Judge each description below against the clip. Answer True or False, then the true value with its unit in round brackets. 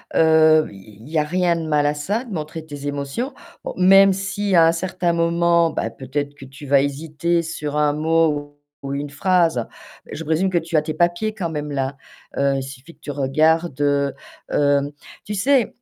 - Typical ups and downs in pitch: True (3.2 semitones)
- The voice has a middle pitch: True (155 Hz)